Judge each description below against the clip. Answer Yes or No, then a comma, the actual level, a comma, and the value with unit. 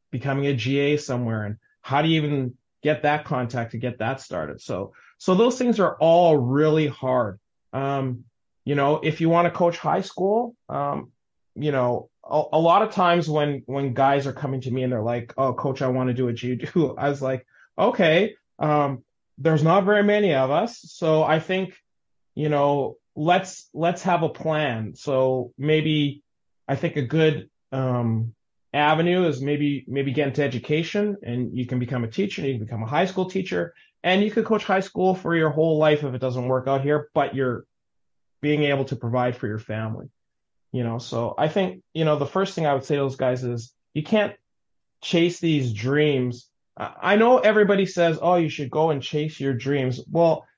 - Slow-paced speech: No, average, 200 wpm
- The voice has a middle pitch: Yes, medium, 145 Hz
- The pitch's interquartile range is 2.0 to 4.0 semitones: No, average, 4.7 semitones